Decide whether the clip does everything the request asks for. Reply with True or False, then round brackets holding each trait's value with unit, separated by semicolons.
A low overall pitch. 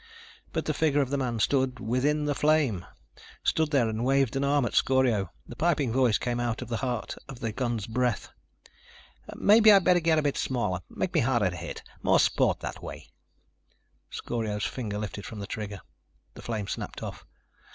True (125 Hz)